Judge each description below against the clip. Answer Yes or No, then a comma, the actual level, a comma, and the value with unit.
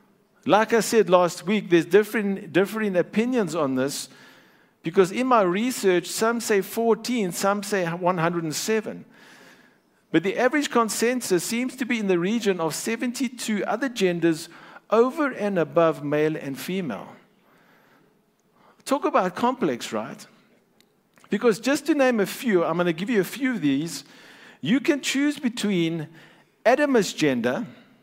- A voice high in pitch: Yes, high, 210 Hz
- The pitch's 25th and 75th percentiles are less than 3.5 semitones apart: No, average, 5.1 semitones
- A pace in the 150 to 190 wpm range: No, average, 140 wpm